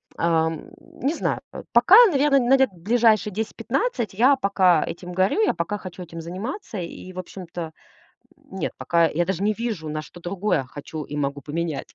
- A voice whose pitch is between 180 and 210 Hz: Yes, medium, 185 Hz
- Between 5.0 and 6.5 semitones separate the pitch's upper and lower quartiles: Yes, wide, 5.6 semitones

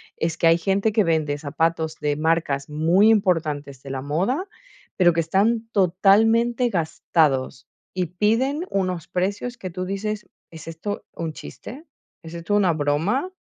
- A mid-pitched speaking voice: Yes, medium, 175 Hz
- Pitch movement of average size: Yes, average, 4.8 semitones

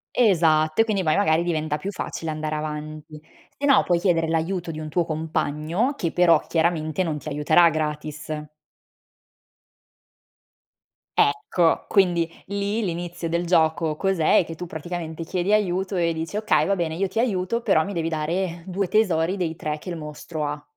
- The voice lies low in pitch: No, medium, 165 Hz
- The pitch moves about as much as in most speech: Yes, average, 3.0 semitones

